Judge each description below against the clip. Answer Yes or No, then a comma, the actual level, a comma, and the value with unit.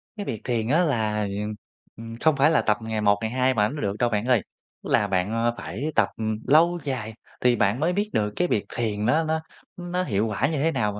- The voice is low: Yes, low, 120 Hz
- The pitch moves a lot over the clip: Yes, wide, 6.4 semitones